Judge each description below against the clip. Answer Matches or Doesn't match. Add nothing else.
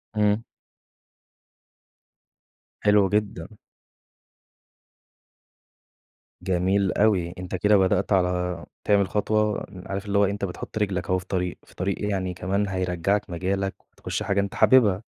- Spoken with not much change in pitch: Matches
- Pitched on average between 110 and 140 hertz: Doesn't match